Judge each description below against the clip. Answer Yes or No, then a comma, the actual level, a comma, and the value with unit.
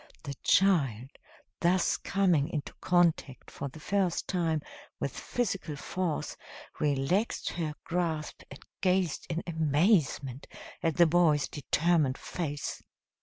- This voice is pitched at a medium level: Yes, medium, 165 Hz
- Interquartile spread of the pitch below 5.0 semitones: Yes, average, 3.6 semitones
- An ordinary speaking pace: No, slow, 115 wpm